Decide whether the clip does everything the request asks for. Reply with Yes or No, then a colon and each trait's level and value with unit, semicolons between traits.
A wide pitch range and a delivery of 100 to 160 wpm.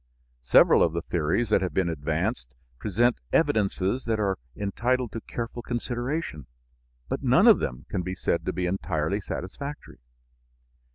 Yes: wide, 5.9 semitones; average, 150 wpm